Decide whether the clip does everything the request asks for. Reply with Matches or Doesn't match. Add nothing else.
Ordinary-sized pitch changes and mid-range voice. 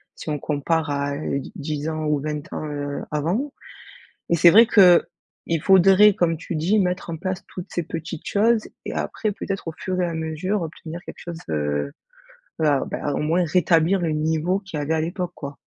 Matches